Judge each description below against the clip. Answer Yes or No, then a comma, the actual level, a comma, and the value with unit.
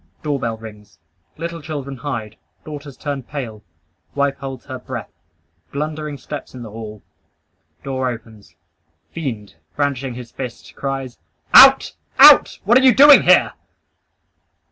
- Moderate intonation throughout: Yes, average, 4.0 semitones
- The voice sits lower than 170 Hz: Yes, low, 135 Hz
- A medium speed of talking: No, slow, 125 wpm